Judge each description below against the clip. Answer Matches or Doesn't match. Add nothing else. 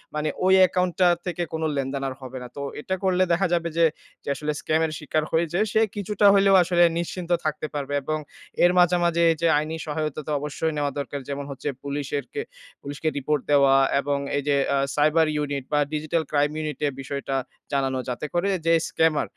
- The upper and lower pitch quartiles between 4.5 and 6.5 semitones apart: Doesn't match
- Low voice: Doesn't match